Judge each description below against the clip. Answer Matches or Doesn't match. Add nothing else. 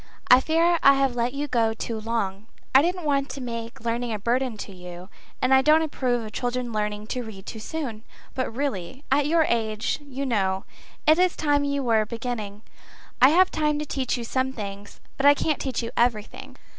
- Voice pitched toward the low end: Doesn't match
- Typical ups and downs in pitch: Matches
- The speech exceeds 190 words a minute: Matches